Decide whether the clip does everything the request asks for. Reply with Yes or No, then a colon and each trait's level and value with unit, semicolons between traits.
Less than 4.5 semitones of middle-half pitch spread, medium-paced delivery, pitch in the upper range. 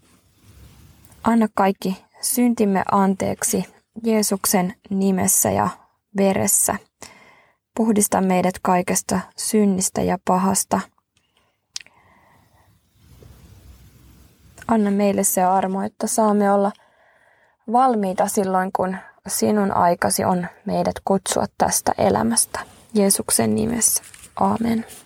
No: average, 2.9 semitones; slow, 80 wpm; high, 200 Hz